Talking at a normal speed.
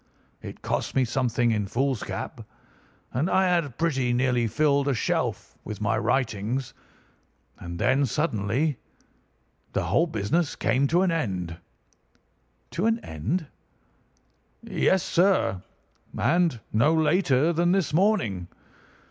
No: slow, 120 wpm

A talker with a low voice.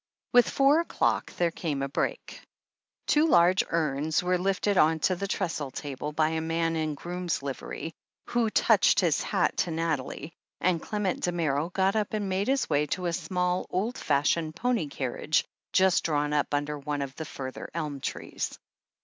No: medium, 165 Hz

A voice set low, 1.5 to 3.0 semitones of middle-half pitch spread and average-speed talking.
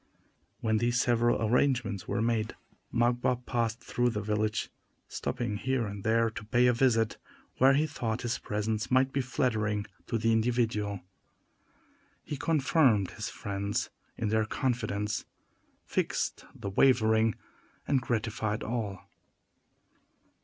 No: low, 115 Hz; narrow, 2.6 semitones; slow, 125 wpm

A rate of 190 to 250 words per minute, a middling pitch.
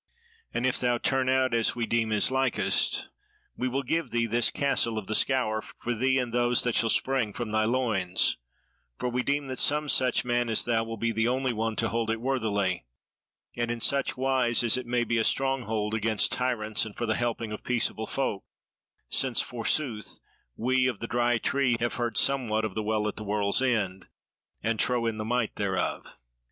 No: average, 200 wpm; low, 120 Hz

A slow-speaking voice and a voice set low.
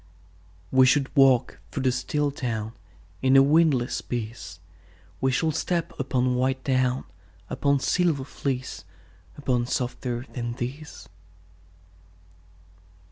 Yes: slow, 110 wpm; low, 130 Hz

